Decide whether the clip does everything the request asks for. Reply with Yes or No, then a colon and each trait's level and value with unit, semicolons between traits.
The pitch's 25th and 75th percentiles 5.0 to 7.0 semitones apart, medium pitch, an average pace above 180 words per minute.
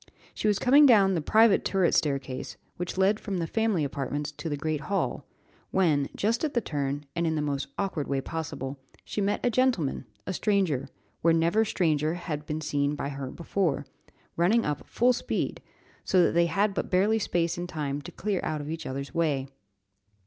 Yes: average, 5.3 semitones; medium, 165 Hz; average, 190 wpm